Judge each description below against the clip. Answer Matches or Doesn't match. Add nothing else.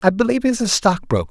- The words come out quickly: Matches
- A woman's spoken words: Doesn't match